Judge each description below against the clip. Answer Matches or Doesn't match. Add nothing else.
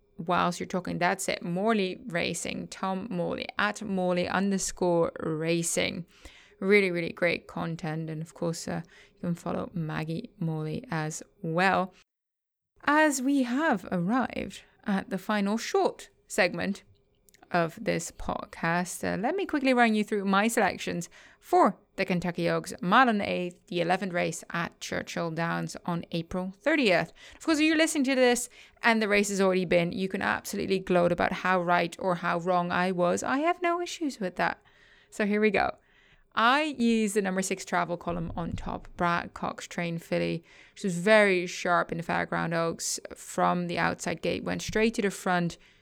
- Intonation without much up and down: Doesn't match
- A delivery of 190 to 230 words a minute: Doesn't match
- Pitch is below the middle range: Doesn't match